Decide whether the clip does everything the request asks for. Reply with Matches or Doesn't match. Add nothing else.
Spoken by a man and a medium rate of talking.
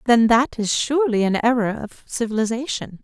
Doesn't match